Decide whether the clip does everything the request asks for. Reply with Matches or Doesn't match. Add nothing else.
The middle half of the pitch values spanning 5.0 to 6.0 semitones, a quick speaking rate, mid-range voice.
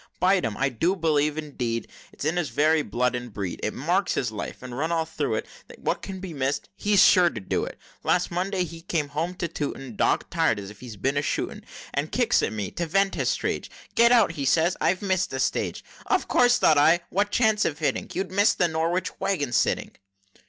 Matches